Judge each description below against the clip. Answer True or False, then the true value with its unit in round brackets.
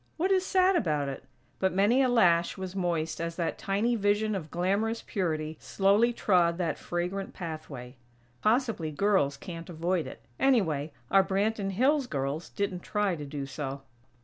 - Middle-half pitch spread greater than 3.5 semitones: True (4.9 semitones)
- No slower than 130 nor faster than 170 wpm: True (160 wpm)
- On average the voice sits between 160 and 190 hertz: True (185 Hz)